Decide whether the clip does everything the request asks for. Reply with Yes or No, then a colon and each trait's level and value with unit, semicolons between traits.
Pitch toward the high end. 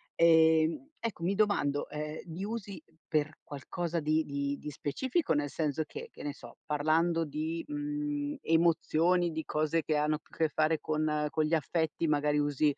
No: medium, 160 Hz